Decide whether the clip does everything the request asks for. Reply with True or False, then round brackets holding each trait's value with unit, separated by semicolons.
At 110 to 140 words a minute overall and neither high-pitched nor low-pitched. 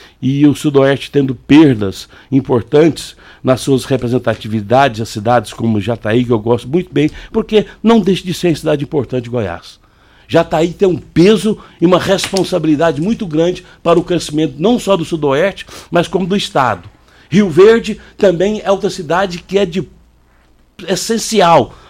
False (160 wpm; 160 Hz)